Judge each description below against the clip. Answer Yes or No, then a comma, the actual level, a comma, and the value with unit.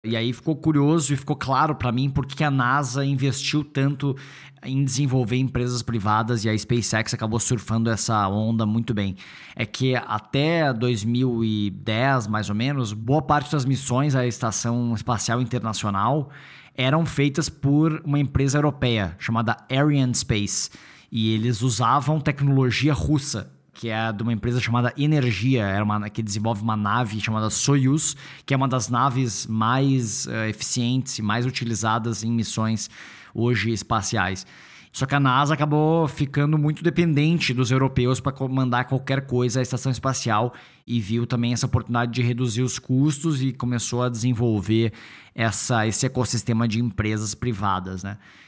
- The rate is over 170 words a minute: No, average, 145 wpm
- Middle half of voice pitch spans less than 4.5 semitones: Yes, average, 3.5 semitones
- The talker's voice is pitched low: Yes, low, 125 Hz